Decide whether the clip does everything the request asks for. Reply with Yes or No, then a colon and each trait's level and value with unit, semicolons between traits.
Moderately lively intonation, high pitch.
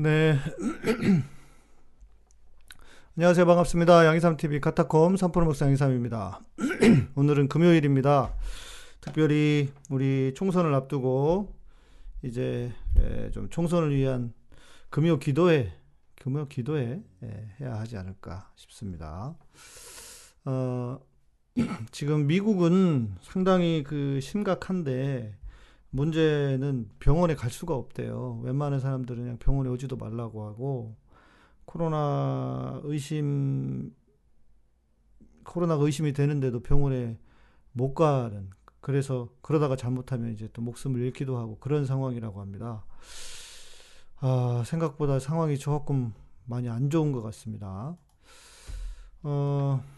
No: average, 5.0 semitones; low, 135 Hz